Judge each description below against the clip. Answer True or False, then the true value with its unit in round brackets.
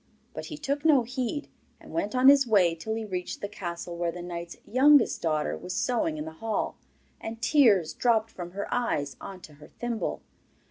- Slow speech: False (195 wpm)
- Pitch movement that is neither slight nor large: False (6.3 semitones)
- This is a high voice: True (210 Hz)